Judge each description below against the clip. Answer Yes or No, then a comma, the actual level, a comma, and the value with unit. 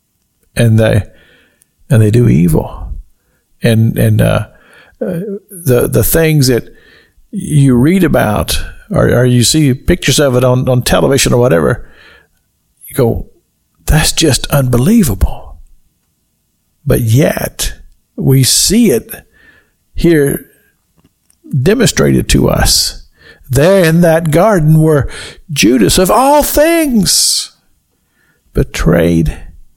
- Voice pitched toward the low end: Yes, low, 125 Hz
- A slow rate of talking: Yes, slow, 105 wpm